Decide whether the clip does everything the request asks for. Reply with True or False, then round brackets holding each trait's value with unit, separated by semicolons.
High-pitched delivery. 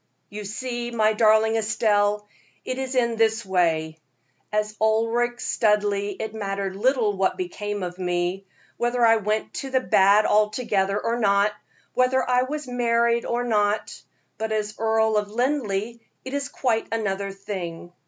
True (215 Hz)